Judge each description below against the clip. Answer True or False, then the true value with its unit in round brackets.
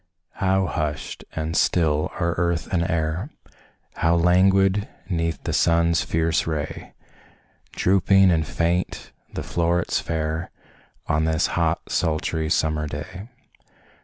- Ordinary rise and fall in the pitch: False (2.2 semitones)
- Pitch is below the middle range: True (85 Hz)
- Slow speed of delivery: True (115 wpm)